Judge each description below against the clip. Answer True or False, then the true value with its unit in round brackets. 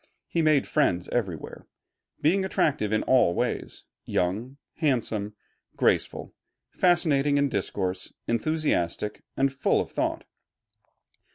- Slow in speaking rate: True (105 wpm)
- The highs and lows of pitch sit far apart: True (6.8 semitones)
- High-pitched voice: False (130 Hz)